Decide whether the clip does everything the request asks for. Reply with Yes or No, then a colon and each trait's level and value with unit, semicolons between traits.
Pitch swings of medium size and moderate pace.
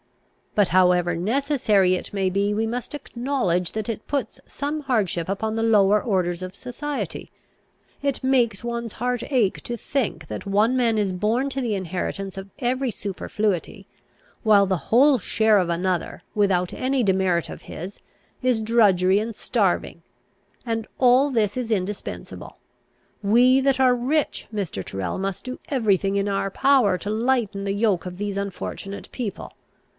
Yes: average, 4.4 semitones; average, 160 wpm